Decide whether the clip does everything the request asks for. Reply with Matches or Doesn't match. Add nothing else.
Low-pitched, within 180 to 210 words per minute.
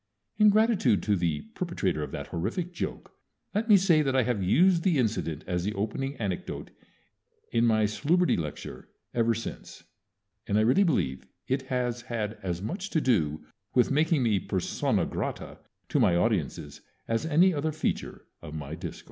Doesn't match